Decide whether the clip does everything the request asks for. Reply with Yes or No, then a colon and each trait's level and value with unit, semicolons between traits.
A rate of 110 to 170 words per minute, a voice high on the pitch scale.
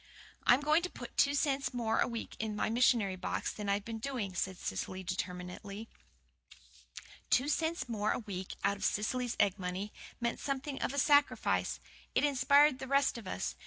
No: average, 180 wpm; high, 230 Hz